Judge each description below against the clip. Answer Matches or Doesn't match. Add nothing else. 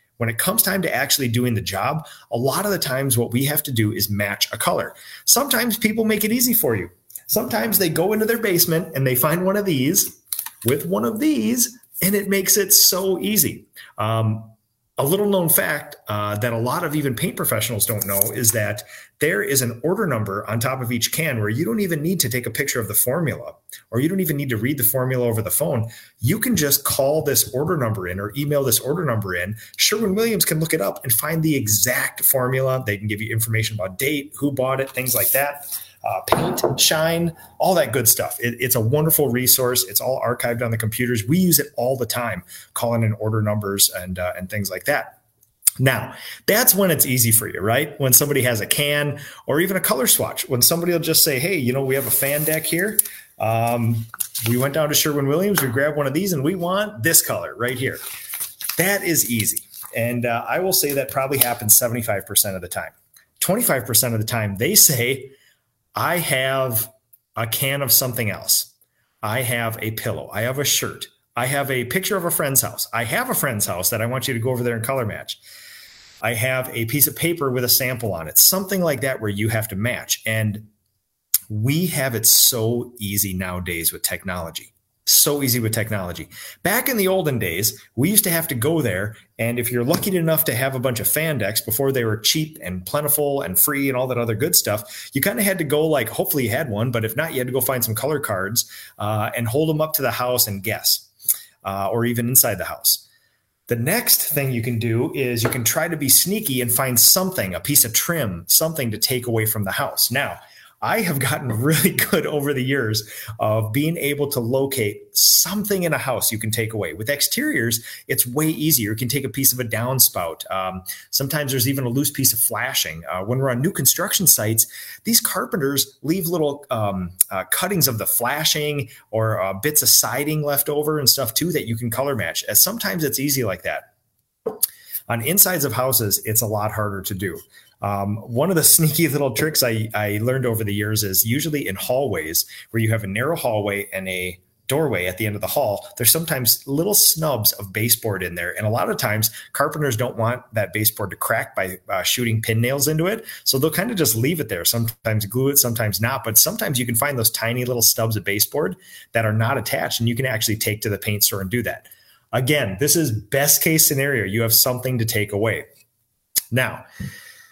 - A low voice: Matches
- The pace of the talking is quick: Matches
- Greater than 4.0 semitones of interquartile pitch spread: Matches